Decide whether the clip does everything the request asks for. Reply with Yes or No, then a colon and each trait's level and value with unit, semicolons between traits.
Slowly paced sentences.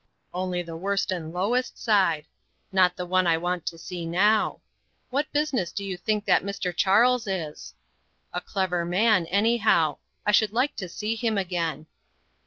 No: average, 165 wpm